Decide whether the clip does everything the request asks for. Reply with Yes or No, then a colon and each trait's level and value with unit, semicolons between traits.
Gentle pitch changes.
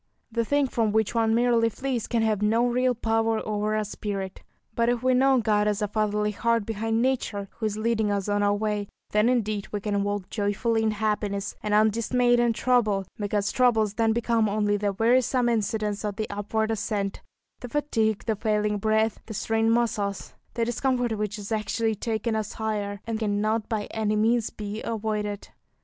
Yes: narrow, 1.8 semitones